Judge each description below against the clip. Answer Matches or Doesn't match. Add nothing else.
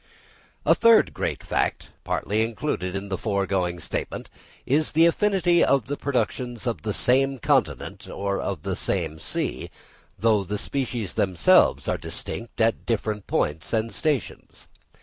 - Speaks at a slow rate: Doesn't match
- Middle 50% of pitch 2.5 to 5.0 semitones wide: Doesn't match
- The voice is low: Matches